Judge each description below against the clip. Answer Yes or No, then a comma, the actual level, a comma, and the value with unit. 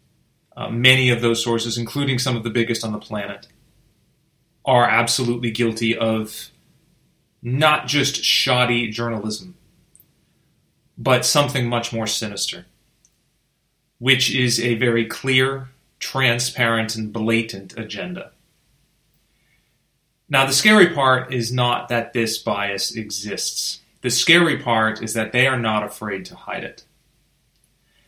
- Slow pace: Yes, slow, 120 wpm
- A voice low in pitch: Yes, low, 120 Hz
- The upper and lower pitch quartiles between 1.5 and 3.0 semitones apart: Yes, average, 2.7 semitones